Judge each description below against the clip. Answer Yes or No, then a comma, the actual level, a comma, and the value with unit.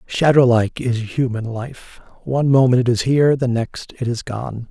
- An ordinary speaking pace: Yes, average, 190 wpm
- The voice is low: Yes, low, 125 Hz